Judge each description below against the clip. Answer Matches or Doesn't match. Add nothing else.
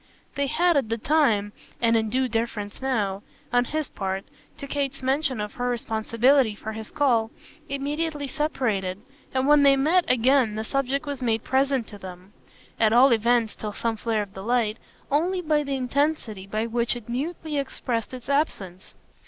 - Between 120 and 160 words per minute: Doesn't match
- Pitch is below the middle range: Doesn't match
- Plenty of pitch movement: Doesn't match